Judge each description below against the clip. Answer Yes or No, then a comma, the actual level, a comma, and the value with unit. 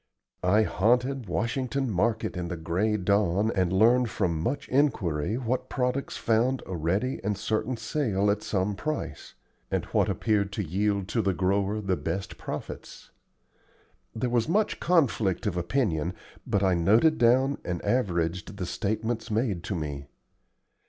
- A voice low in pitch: Yes, low, 105 Hz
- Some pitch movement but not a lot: Yes, average, 4.9 semitones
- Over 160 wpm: No, average, 150 wpm